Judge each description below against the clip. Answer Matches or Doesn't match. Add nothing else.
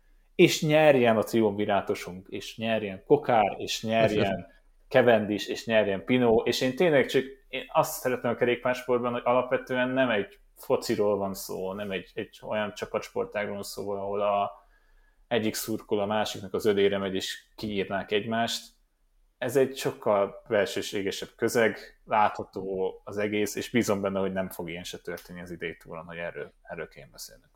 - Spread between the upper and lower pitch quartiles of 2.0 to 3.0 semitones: Doesn't match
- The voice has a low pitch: Matches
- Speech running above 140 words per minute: Matches